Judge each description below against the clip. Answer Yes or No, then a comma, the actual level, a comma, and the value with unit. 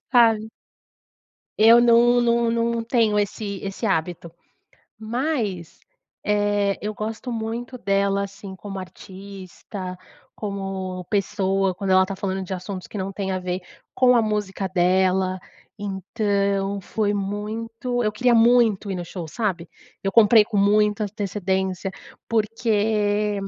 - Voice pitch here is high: Yes, high, 205 Hz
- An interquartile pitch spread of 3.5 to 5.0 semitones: No, average, 2.7 semitones